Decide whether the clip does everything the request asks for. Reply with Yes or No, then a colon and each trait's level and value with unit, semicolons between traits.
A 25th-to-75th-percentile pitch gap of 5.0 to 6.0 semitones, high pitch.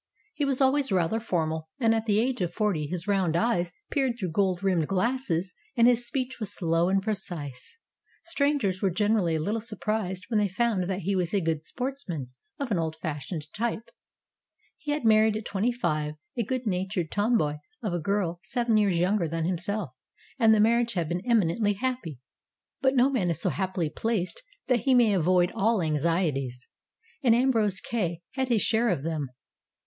Yes: wide, 5.4 semitones; high, 200 Hz